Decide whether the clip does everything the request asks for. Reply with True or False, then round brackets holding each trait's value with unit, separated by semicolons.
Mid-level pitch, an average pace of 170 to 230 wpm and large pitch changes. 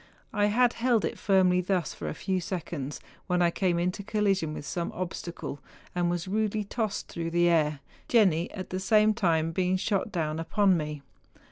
False (180 Hz; 180 wpm; 3.4 semitones)